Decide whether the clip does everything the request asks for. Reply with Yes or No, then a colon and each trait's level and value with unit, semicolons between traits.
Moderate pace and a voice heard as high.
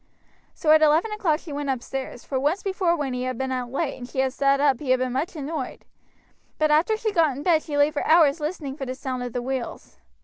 No: fast, 250 wpm; very high, 285 Hz